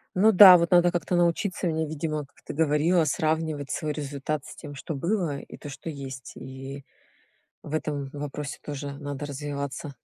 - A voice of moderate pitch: Yes, medium, 150 Hz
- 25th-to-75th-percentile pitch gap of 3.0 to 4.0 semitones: No, narrow, 2.6 semitones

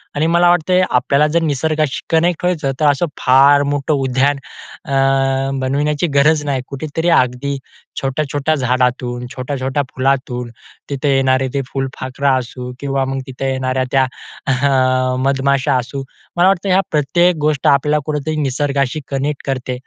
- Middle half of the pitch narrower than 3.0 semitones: Yes, narrow, 2.5 semitones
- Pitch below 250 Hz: Yes, medium, 140 Hz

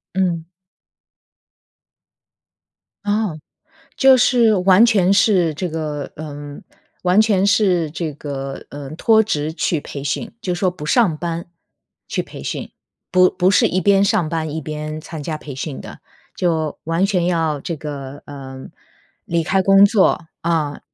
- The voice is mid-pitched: Yes, medium, 170 Hz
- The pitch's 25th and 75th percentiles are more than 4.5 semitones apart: No, average, 4.2 semitones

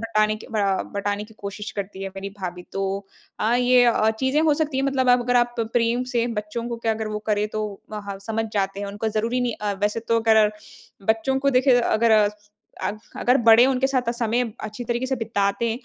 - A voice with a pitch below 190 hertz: No, high, 225 Hz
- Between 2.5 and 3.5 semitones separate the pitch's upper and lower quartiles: Yes, average, 2.9 semitones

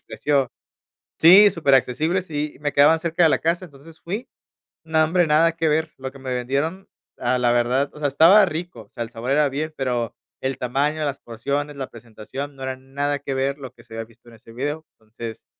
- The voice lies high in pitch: No, medium, 140 Hz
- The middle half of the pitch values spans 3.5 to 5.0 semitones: Yes, average, 3.9 semitones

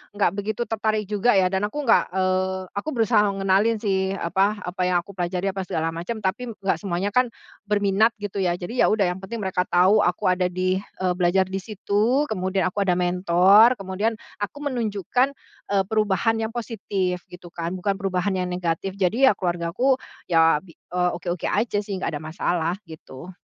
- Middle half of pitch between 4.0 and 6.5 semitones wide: No, average, 2.8 semitones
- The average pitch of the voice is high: Yes, high, 195 Hz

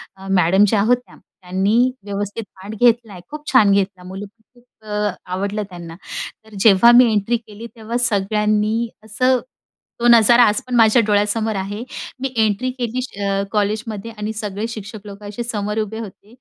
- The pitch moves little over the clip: Yes, narrow, 2.3 semitones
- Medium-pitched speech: No, high, 210 Hz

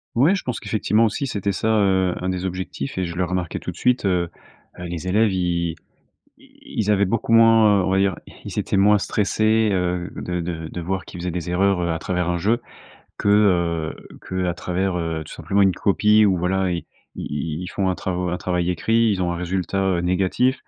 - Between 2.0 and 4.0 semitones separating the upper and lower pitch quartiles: Yes, average, 2.7 semitones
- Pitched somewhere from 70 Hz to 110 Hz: Yes, very low, 95 Hz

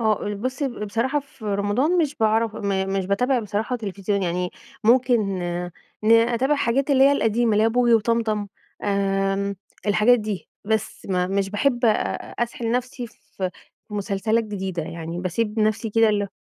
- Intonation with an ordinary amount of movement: Yes, average, 3.2 semitones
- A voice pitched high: Yes, high, 215 Hz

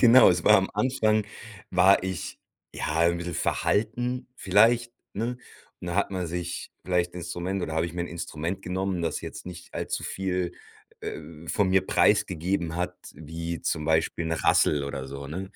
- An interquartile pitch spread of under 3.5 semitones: Yes, average, 2.7 semitones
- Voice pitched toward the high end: No, very low, 90 Hz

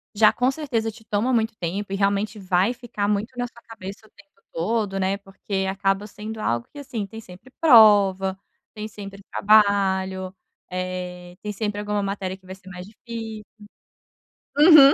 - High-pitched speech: Yes, high, 205 Hz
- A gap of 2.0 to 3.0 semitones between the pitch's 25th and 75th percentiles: Yes, narrow, 2.6 semitones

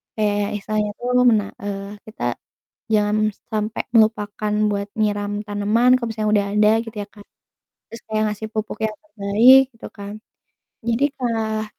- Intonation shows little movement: Yes, narrow, 1.5 semitones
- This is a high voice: Yes, high, 215 Hz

